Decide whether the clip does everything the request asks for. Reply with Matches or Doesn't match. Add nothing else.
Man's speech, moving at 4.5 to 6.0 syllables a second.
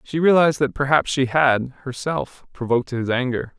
Matches